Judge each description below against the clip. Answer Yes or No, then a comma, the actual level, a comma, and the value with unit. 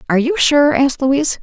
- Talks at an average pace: No, fast, 210 wpm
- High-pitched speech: Yes, very high, 275 Hz